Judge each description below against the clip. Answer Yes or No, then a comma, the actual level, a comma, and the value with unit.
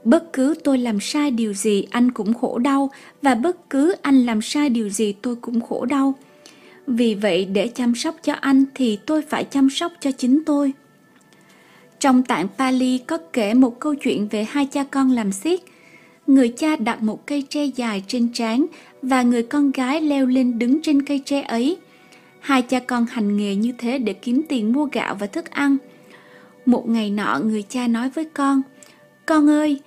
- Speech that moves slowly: No, average, 195 wpm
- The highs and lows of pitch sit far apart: No, average, 3.5 semitones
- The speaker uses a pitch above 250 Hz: Yes, very high, 260 Hz